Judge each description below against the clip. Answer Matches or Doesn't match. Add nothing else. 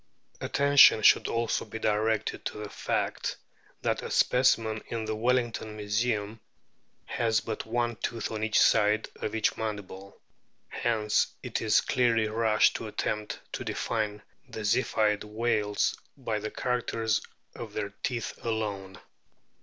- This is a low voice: Matches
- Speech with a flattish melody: Matches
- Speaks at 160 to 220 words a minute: Doesn't match